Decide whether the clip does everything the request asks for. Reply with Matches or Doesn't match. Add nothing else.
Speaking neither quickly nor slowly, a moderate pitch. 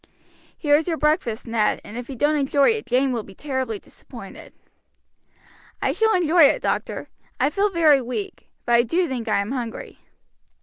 Doesn't match